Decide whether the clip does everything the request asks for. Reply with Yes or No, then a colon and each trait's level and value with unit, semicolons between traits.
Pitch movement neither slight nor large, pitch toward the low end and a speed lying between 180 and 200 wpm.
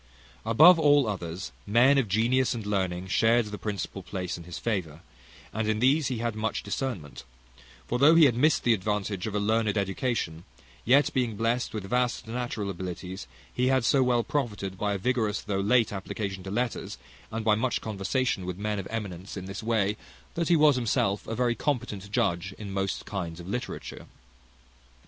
Yes: average, 4.2 semitones; low, 110 Hz; average, 185 wpm